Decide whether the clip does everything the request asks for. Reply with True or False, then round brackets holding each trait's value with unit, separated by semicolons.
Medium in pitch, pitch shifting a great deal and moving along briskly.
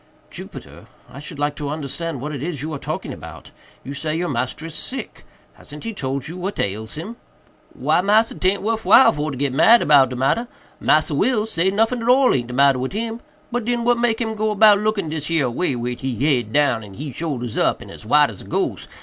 True (155 Hz; 7.9 semitones; 225 wpm)